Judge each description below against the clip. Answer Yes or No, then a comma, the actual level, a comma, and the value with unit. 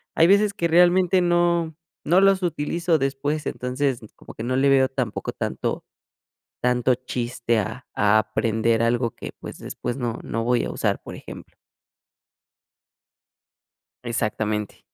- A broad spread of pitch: Yes, wide, 6.3 semitones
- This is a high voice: No, low, 130 Hz